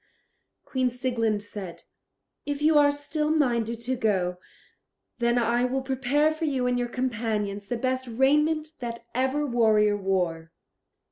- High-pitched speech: Yes, high, 245 Hz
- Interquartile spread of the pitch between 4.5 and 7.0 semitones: No, average, 3.6 semitones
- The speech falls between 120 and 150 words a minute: Yes, average, 140 wpm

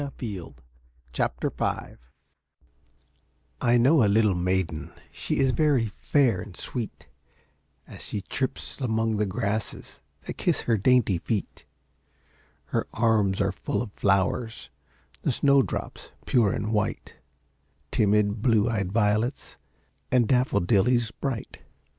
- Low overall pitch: Yes, low, 110 Hz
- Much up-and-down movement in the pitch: No, average, 3.6 semitones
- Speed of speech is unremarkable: No, slow, 125 wpm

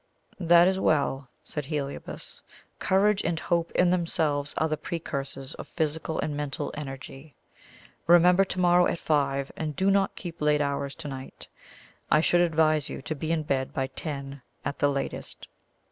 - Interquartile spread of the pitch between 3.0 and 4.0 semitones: Yes, average, 3.5 semitones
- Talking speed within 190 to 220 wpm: No, average, 165 wpm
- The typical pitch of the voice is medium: Yes, medium, 155 Hz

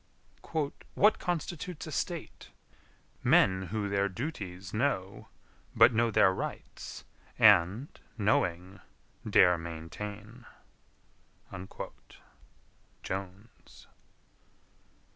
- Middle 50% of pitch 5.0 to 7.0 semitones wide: No, average, 4.1 semitones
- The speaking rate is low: Yes, slow, 70 wpm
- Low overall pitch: Yes, low, 100 Hz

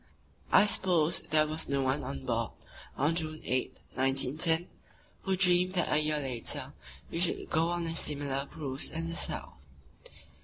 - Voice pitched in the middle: Yes, medium, 155 Hz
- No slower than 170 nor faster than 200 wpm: No, average, 160 wpm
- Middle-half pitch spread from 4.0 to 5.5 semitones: No, average, 3.4 semitones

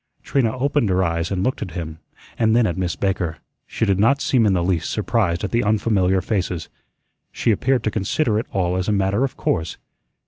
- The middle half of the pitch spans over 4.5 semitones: No, average, 4.0 semitones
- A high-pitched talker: No, low, 100 Hz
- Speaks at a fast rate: Yes, fast, 210 wpm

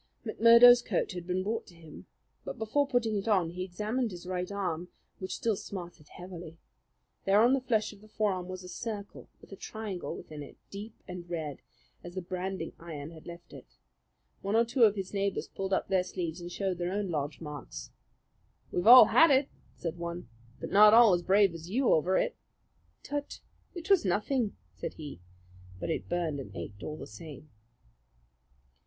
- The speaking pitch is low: No, medium, 185 Hz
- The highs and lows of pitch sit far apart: No, average, 4.0 semitones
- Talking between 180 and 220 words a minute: Yes, average, 190 wpm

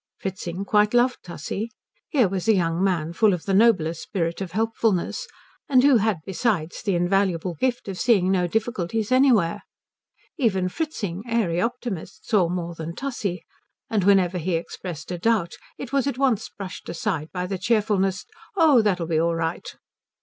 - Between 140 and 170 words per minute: Yes, average, 165 wpm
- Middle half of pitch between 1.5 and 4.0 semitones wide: No, average, 4.6 semitones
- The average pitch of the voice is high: Yes, high, 195 Hz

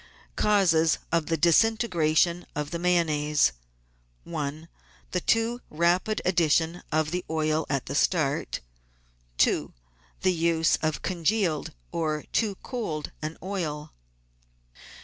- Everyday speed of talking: No, slow, 115 wpm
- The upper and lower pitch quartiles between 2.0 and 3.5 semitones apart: Yes, average, 2.8 semitones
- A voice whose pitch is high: No, medium, 165 Hz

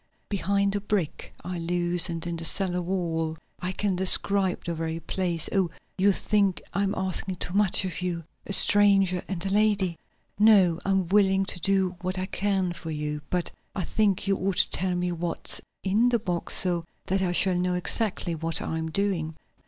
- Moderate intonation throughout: No, narrow, 2.3 semitones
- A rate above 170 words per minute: Yes, average, 190 wpm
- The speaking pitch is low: No, medium, 185 Hz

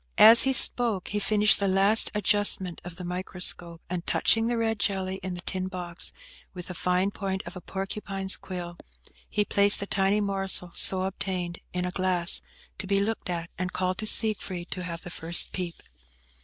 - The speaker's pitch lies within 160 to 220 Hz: Yes, high, 190 Hz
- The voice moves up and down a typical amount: No, narrow, 2.0 semitones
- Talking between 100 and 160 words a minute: No, average, 185 wpm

